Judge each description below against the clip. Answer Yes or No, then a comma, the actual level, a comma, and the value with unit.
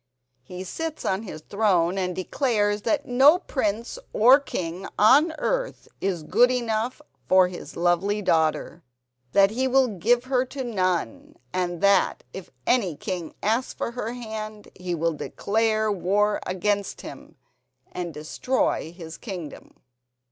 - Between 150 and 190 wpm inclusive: No, average, 140 wpm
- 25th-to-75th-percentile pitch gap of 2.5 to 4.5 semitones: No, average, 5.3 semitones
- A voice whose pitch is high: Yes, high, 205 Hz